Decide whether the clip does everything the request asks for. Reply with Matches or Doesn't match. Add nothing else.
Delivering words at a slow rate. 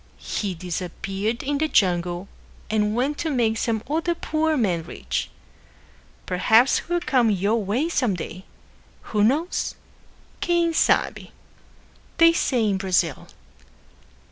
Matches